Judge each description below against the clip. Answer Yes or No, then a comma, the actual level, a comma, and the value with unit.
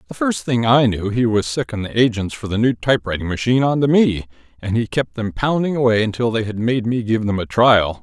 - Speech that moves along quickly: Yes, fast, 245 wpm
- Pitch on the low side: Yes, low, 115 Hz